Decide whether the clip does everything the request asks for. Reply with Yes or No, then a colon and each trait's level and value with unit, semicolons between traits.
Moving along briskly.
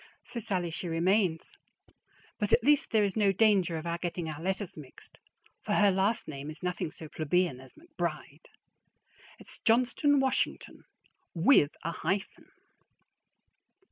No: average, 140 wpm